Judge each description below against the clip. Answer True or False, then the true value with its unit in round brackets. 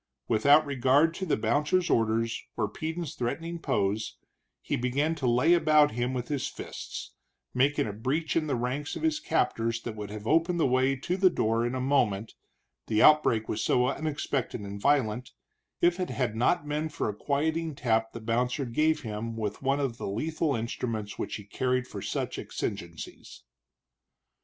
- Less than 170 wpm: False (175 wpm)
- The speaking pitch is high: False (130 Hz)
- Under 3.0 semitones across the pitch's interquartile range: False (5.2 semitones)